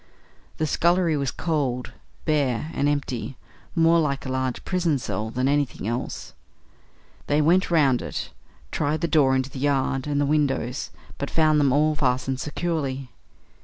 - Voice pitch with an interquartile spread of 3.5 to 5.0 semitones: No, average, 2.9 semitones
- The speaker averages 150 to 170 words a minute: Yes, average, 155 wpm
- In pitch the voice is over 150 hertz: No, medium, 145 Hz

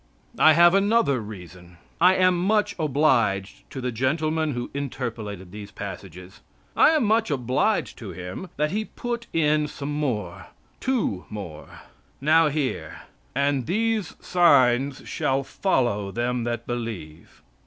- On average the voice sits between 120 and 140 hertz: Yes, low, 135 Hz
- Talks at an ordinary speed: No, slow, 130 wpm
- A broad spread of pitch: Yes, wide, 7.8 semitones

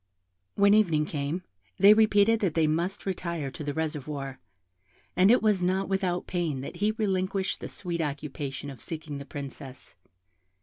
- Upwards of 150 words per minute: Yes, average, 160 wpm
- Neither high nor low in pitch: Yes, medium, 170 Hz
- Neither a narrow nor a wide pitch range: Yes, average, 5.0 semitones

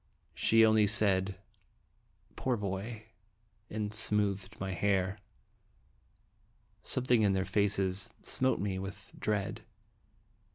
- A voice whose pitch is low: Yes, low, 100 Hz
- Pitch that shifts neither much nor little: No, narrow, 2.1 semitones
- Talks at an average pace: No, slow, 95 wpm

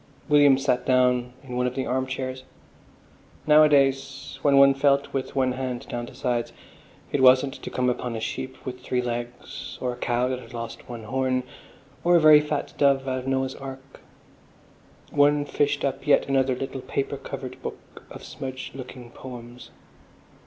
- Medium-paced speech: Yes, average, 175 wpm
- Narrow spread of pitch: Yes, narrow, 1.6 semitones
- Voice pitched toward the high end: No, low, 130 Hz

